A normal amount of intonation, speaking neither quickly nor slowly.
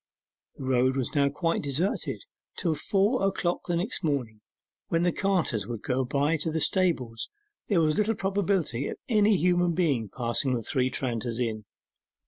No: wide, 6.2 semitones; average, 165 wpm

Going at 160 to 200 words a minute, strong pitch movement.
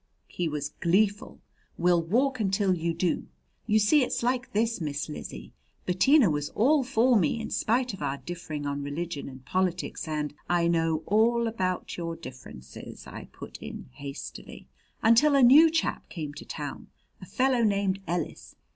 Yes: average, 165 wpm; wide, 6.6 semitones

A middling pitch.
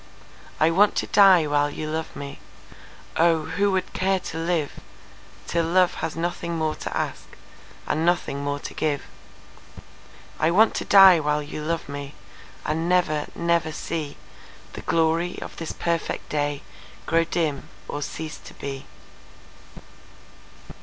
Yes: medium, 160 Hz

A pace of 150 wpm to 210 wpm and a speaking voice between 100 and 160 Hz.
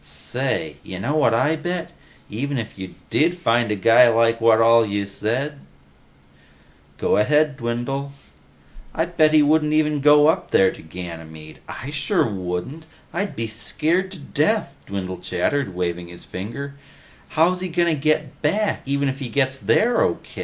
Yes: average, 170 wpm; low, 135 Hz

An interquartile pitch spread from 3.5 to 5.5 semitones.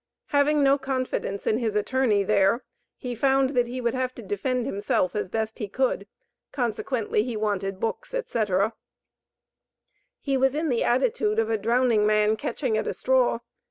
Yes: average, 3.9 semitones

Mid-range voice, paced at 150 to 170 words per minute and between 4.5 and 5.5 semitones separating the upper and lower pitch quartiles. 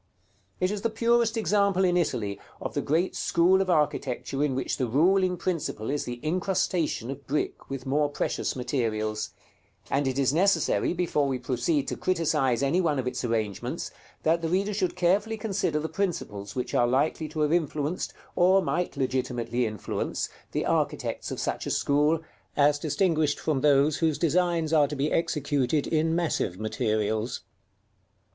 Yes: medium, 150 Hz; average, 165 wpm; average, 5.2 semitones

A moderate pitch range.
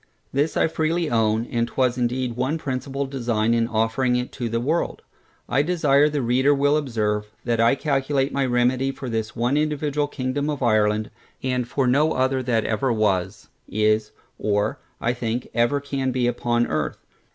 Yes: average, 3.2 semitones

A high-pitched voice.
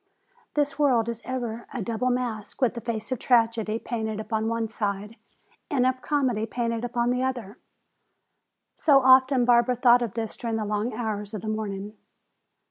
Yes: high, 235 Hz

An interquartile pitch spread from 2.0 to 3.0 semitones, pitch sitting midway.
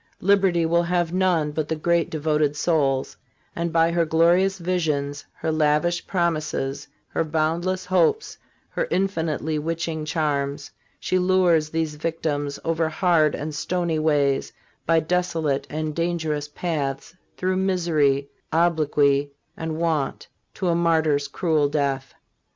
Yes: narrow, 2.5 semitones; medium, 160 Hz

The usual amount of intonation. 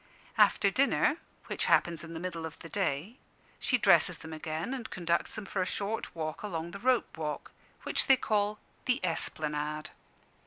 Yes: average, 4.8 semitones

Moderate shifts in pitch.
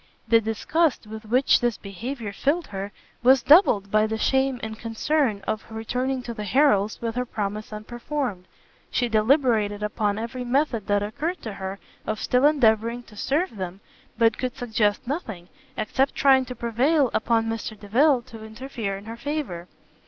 Yes: average, 3.8 semitones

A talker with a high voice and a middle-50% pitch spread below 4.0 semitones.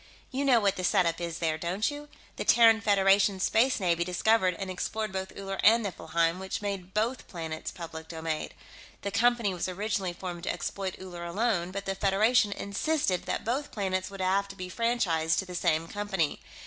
Yes: high, 195 Hz; average, 3.6 semitones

